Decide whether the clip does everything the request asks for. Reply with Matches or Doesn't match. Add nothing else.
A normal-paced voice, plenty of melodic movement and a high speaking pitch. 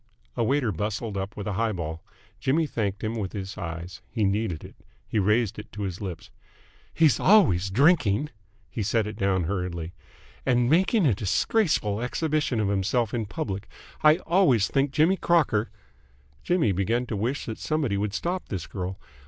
Doesn't match